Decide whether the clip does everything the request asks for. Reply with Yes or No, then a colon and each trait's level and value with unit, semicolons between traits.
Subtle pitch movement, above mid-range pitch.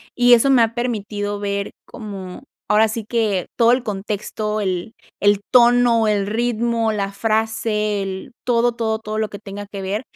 Yes: narrow, 2.3 semitones; high, 215 Hz